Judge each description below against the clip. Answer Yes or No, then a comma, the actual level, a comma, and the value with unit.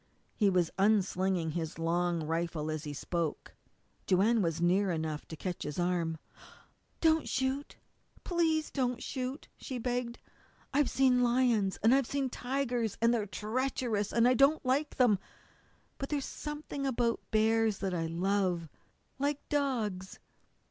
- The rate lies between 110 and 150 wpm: Yes, average, 140 wpm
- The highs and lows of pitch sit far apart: Yes, wide, 6.7 semitones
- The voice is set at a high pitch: Yes, high, 220 Hz